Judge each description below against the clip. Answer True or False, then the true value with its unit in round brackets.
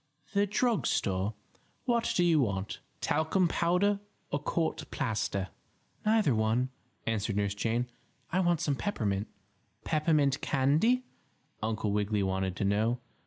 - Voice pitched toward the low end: True (130 Hz)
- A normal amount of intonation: False (8.9 semitones)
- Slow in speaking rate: True (125 wpm)